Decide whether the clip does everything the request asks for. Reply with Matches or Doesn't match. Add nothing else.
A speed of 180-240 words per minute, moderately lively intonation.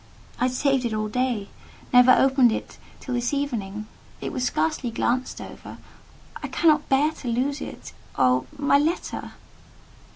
Doesn't match